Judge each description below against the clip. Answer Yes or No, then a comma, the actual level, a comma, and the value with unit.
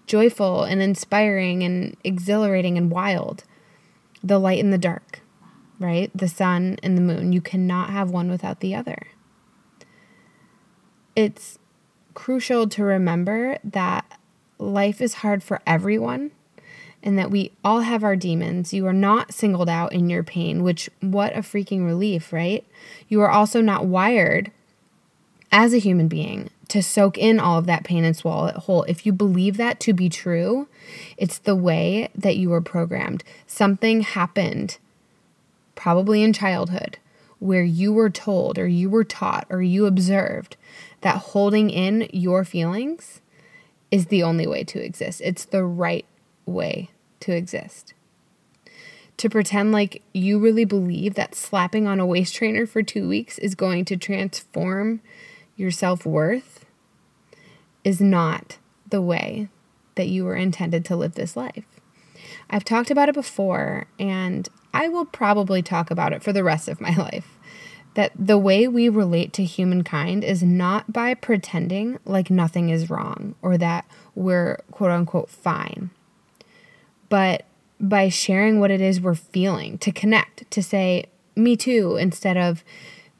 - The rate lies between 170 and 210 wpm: No, average, 155 wpm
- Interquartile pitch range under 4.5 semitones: Yes, average, 2.9 semitones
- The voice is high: Yes, high, 195 Hz